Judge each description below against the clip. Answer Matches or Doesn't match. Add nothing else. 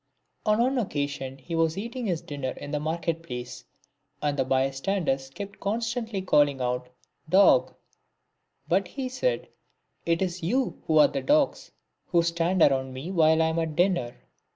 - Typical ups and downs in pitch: Doesn't match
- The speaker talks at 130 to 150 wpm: Doesn't match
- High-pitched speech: Doesn't match